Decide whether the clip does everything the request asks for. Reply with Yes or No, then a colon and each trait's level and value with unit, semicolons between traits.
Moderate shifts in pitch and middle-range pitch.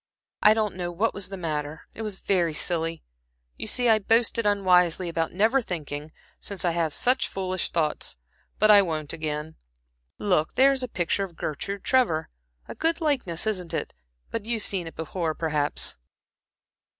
Yes: average, 4.8 semitones; medium, 180 Hz